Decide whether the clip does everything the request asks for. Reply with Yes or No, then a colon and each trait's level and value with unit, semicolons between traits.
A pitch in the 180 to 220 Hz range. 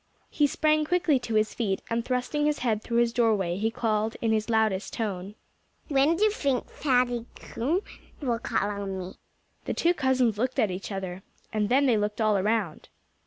No: high, 230 Hz